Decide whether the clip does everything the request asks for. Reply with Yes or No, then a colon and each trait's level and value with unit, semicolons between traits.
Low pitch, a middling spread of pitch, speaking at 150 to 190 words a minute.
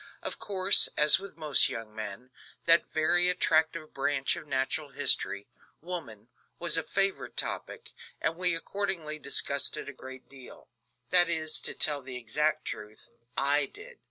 No: medium, 155 Hz; average, 4.7 semitones; average, 155 wpm